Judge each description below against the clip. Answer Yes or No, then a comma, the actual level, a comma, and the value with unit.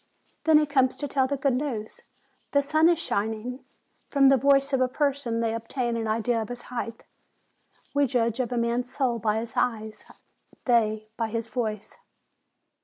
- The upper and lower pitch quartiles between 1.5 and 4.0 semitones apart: Yes, average, 3.3 semitones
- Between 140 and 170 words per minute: No, average, 180 wpm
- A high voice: Yes, high, 245 Hz